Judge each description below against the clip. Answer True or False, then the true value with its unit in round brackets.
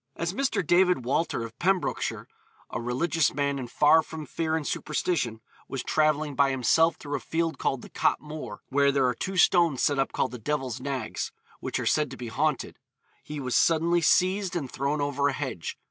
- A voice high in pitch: False (145 Hz)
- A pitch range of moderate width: True (3.7 semitones)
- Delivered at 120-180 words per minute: False (195 wpm)